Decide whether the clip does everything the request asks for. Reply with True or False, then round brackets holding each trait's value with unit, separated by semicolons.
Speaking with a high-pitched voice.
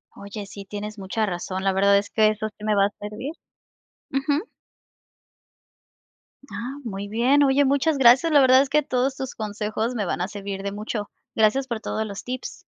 True (215 Hz)